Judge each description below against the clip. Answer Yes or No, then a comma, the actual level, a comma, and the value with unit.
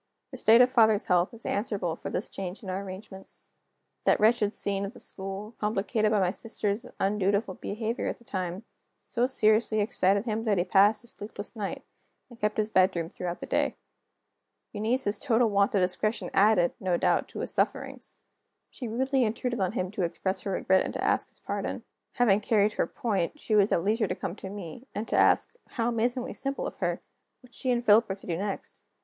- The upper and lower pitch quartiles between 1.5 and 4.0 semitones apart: Yes, average, 2.9 semitones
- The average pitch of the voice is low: No, high, 210 Hz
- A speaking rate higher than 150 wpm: Yes, fast, 205 wpm